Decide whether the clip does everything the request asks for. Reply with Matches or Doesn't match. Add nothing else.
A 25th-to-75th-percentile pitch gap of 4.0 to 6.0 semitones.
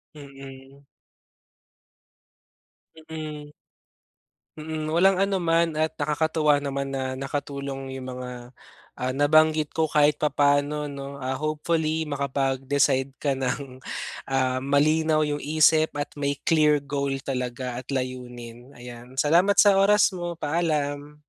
Doesn't match